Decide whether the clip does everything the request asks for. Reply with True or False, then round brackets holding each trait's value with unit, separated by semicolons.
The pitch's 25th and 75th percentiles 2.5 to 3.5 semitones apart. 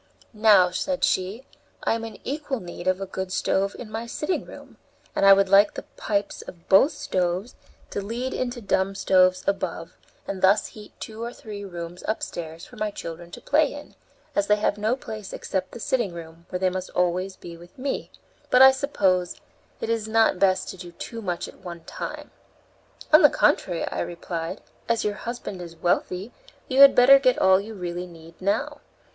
False (4.1 semitones)